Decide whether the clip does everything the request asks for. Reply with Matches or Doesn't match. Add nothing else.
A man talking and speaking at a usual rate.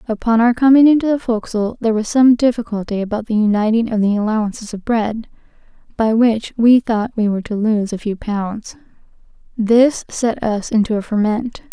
Doesn't match